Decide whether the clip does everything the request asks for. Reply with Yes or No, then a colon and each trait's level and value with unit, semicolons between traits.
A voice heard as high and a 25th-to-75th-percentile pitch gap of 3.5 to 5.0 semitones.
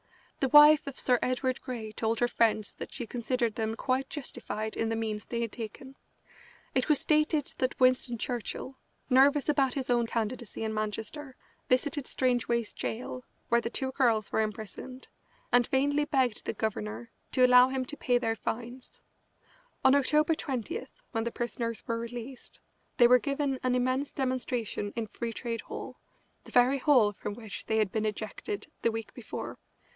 No: high, 245 Hz; average, 2.8 semitones